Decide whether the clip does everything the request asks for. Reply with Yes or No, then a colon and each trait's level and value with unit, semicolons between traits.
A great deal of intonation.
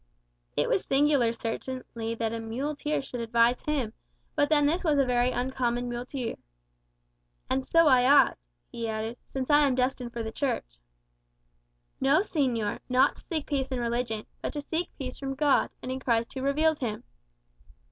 No: average, 3.3 semitones